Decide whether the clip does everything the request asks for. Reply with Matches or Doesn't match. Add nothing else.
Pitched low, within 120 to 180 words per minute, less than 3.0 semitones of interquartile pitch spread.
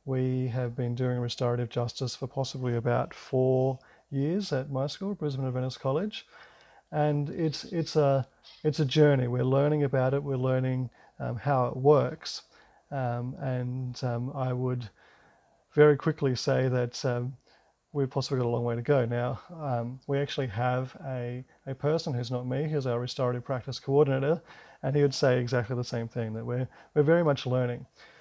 Matches